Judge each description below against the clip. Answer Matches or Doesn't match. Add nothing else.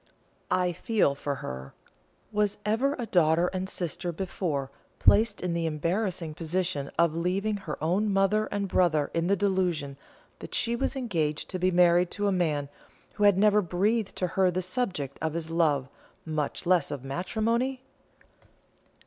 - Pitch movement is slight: Doesn't match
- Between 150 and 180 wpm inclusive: Matches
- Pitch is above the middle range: Doesn't match